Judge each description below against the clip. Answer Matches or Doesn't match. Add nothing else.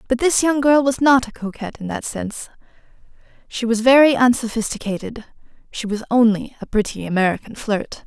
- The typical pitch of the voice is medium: Doesn't match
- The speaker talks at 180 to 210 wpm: Doesn't match